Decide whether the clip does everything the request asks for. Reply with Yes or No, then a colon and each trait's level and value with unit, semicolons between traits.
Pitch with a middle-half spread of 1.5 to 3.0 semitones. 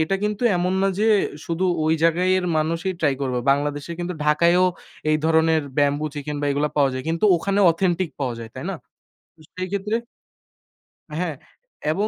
No: average, 3.7 semitones